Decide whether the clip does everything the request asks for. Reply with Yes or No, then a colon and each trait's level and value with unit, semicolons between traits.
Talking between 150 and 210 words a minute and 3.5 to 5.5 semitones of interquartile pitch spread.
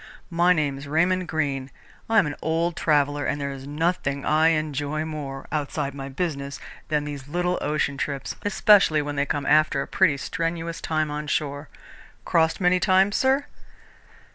No: average, 160 wpm; average, 2.9 semitones